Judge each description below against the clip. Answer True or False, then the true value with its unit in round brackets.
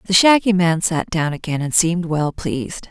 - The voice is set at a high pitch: False (175 Hz)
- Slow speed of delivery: False (205 wpm)